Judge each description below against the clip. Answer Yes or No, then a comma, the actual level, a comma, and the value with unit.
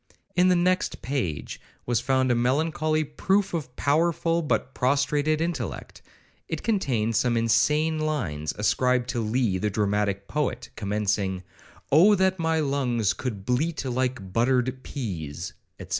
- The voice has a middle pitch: No, low, 130 Hz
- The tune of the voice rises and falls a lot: Yes, wide, 6.1 semitones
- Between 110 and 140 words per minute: Yes, slow, 135 wpm